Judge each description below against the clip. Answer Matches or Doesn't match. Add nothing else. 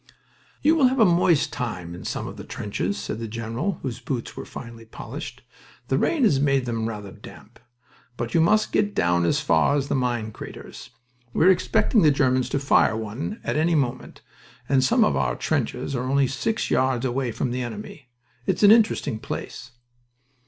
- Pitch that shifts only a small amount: Doesn't match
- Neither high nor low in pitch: Doesn't match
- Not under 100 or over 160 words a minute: Doesn't match